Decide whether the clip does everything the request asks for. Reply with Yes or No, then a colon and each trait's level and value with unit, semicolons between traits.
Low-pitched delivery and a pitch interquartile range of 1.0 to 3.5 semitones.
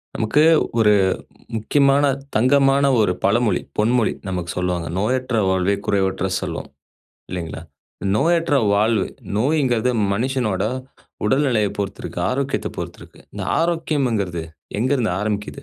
No: low, 115 Hz; average, 5.3 semitones